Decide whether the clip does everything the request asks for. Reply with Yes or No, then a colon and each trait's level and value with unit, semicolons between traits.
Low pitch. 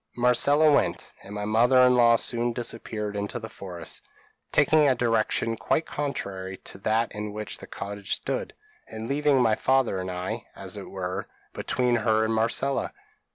Yes: low, 115 Hz